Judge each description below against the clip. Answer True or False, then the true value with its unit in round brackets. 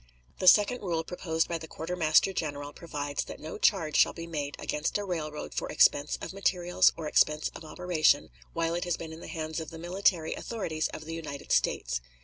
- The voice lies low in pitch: False (160 Hz)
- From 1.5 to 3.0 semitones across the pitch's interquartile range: True (2.4 semitones)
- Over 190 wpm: True (200 wpm)